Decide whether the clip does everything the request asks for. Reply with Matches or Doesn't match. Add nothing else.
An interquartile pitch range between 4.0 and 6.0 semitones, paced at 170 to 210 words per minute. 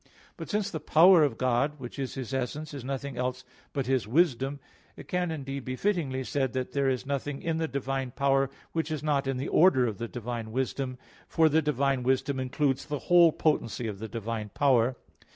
Doesn't match